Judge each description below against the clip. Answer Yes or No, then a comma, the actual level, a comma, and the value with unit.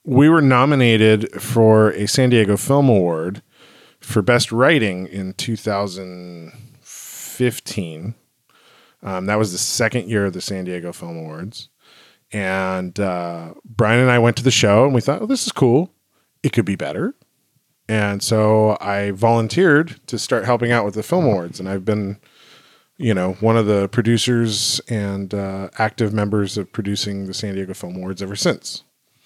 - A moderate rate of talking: Yes, average, 165 wpm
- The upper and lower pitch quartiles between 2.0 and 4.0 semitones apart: Yes, average, 3.3 semitones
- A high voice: No, low, 105 Hz